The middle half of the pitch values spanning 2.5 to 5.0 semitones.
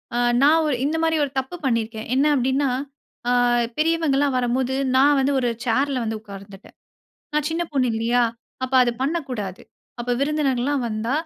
Yes: average, 3.4 semitones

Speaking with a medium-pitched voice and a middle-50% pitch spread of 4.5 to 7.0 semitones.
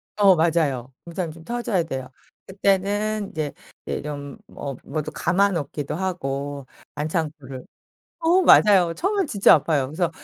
Yes: medium, 165 Hz; wide, 5.6 semitones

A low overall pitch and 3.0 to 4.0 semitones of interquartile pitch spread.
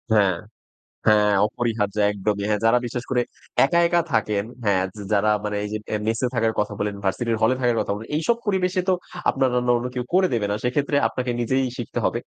Yes: low, 115 Hz; average, 3.5 semitones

